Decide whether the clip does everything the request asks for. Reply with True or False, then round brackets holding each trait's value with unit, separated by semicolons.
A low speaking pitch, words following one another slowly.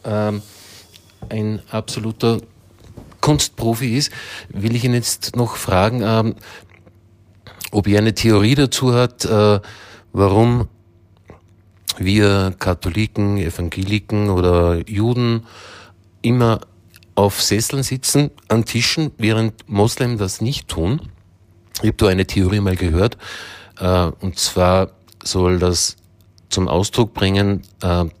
True (105 Hz; 110 wpm)